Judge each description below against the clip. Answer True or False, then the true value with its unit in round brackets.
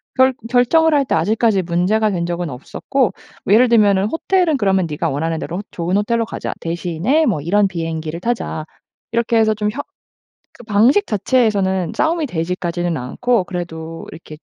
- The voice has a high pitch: True (200 Hz)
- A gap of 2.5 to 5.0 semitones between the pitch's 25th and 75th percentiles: False (5.6 semitones)